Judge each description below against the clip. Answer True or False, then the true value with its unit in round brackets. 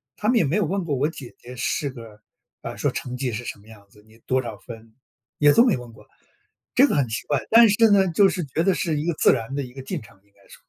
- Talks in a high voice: False (135 Hz)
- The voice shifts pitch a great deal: True (7.3 semitones)